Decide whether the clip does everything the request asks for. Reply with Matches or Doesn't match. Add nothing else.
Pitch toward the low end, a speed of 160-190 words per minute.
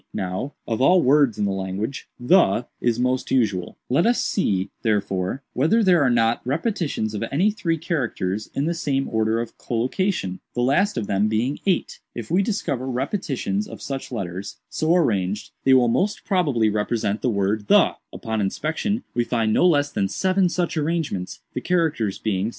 Matches